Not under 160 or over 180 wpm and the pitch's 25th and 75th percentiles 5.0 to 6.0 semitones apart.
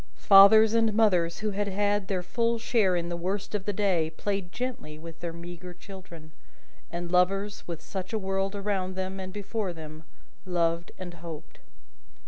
No: average, 170 wpm; average, 3.1 semitones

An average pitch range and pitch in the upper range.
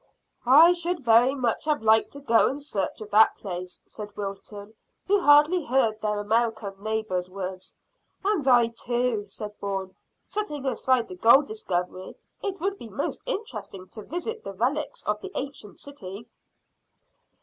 No: wide, 5.7 semitones; high, 230 Hz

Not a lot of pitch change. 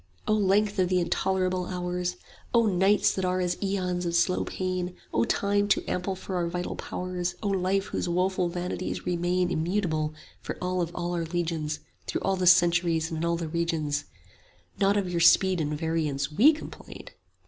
Yes: narrow, 1.8 semitones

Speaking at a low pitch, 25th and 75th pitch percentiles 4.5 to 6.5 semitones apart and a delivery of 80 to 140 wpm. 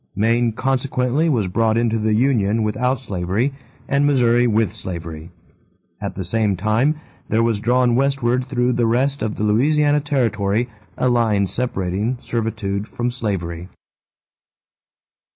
No: low, 115 Hz; average, 3.3 semitones; slow, 135 wpm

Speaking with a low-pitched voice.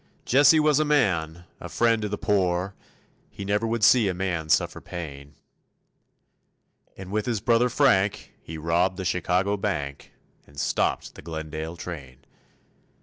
Yes: very low, 95 Hz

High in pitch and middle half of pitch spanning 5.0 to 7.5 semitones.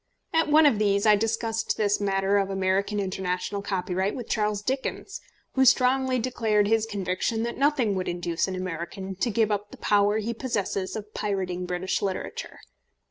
No: high, 205 Hz; average, 2.9 semitones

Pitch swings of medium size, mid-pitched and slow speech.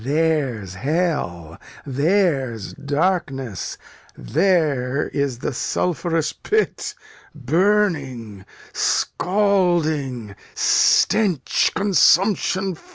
No: wide, 6.1 semitones; medium, 150 Hz; slow, 55 wpm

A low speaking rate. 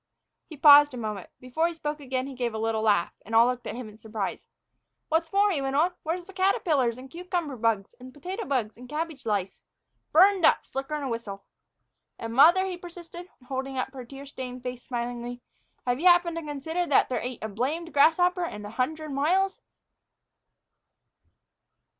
No: average, 195 wpm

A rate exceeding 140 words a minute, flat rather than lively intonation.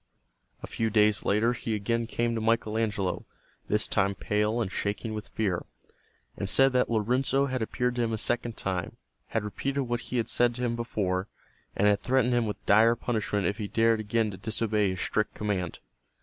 Yes: average, 195 wpm; narrow, 2.3 semitones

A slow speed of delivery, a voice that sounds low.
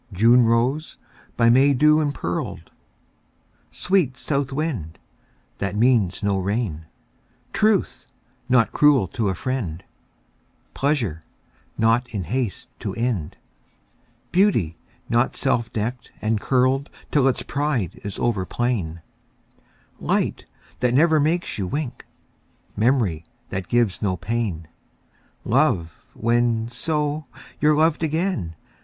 Yes: slow, 110 wpm; low, 120 Hz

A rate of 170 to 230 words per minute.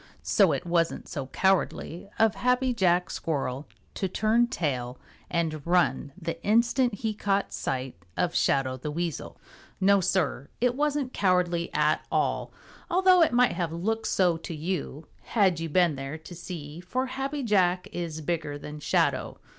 No: average, 155 wpm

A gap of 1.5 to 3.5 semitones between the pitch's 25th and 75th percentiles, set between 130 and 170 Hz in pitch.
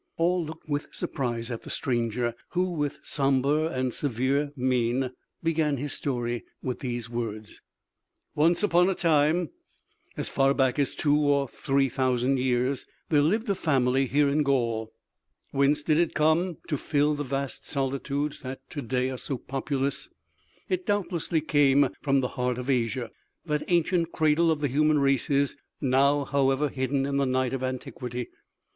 Yes: average, 2.7 semitones; medium, 140 Hz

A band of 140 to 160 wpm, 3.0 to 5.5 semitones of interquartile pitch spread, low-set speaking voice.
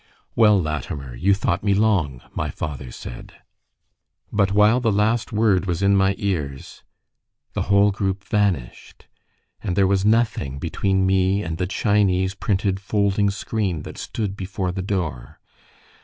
No: average, 145 wpm; narrow, 2.6 semitones; very low, 95 Hz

